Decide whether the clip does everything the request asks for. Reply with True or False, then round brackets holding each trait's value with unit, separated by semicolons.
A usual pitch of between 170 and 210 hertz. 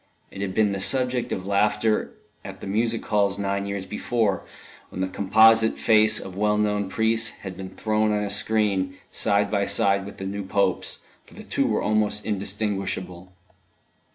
False (100 Hz)